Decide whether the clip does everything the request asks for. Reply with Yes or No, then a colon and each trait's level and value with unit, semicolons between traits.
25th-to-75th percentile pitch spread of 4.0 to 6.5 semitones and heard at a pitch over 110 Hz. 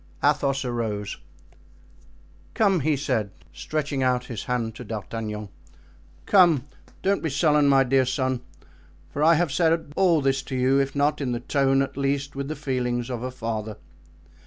No: average, 3.2 semitones; low, 135 Hz